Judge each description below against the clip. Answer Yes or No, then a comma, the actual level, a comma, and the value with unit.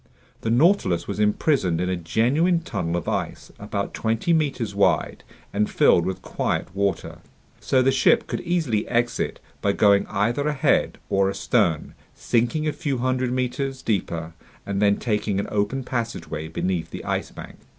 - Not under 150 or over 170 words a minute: Yes, average, 160 wpm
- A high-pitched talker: No, low, 110 Hz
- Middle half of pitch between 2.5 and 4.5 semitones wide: No, average, 5.1 semitones